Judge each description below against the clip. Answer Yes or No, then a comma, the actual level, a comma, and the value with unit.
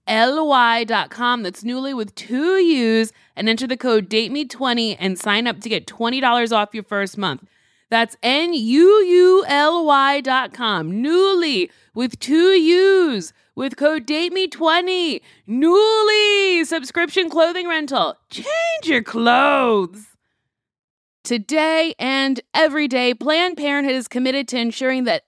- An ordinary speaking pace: No, slow, 125 wpm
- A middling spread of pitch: No, wide, 5.9 semitones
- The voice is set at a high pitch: Yes, very high, 265 Hz